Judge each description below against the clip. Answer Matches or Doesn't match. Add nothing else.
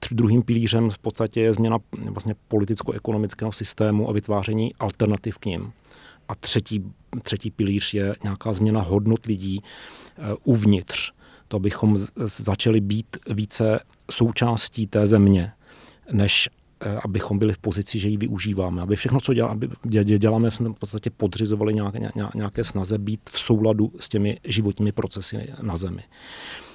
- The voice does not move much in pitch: Matches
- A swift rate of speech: Doesn't match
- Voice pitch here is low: Matches